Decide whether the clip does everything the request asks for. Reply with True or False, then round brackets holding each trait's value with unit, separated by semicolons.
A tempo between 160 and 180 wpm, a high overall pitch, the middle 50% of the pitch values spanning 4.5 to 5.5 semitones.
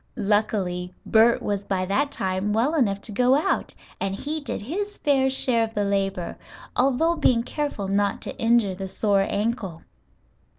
True (165 wpm; 215 Hz; 5.1 semitones)